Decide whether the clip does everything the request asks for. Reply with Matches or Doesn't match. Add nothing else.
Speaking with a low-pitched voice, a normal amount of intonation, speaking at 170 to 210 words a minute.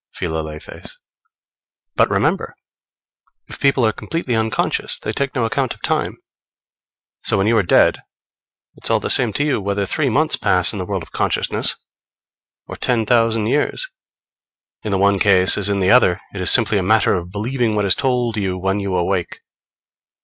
Matches